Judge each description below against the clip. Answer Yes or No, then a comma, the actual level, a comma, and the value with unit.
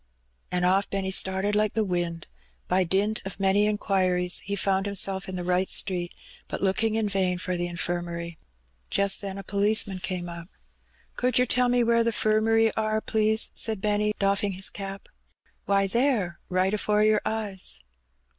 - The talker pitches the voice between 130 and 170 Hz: No, high, 195 Hz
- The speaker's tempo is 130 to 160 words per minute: No, average, 170 wpm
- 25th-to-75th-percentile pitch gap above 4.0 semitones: No, average, 2.7 semitones